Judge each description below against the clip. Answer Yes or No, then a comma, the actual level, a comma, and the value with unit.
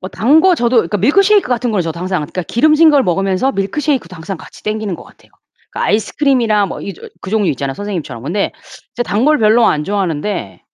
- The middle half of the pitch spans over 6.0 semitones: No, wide, 5.5 semitones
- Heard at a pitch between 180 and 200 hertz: No, high, 210 Hz